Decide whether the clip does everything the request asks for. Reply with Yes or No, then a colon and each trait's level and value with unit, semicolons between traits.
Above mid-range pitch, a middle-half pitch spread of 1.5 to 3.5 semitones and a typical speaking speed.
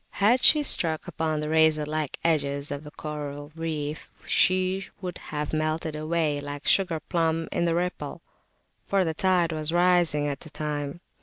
No: medium, 160 Hz; narrow, 2.4 semitones; average, 175 wpm